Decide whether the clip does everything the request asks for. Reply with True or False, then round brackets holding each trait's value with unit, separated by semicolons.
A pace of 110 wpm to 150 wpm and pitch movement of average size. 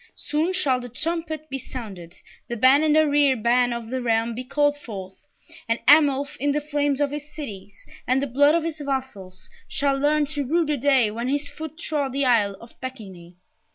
False (195 wpm; 3.9 semitones)